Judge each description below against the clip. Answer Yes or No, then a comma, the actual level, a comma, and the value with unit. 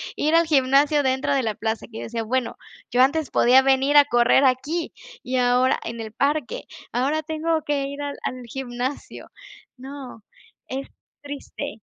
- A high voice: Yes, very high, 265 Hz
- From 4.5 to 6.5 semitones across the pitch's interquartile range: No, average, 2.7 semitones